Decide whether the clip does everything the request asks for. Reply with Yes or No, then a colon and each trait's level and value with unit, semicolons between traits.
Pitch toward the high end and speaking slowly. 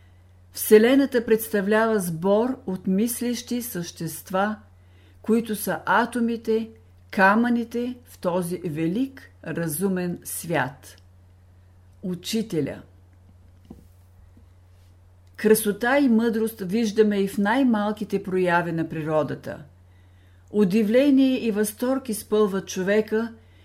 Yes: high, 195 Hz; slow, 80 wpm